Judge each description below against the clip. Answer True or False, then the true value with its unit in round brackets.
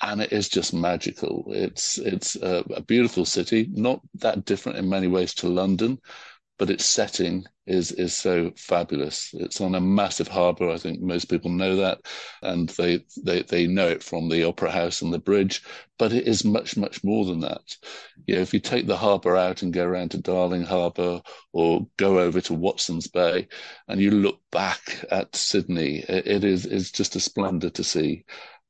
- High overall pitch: False (90 Hz)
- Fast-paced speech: False (190 wpm)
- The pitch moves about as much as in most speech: False (2.2 semitones)